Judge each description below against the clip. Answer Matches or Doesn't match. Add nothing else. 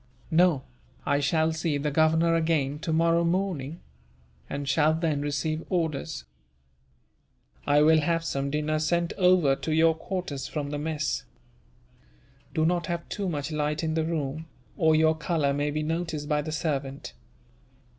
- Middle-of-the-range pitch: Matches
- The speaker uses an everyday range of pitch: Doesn't match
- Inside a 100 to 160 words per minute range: Matches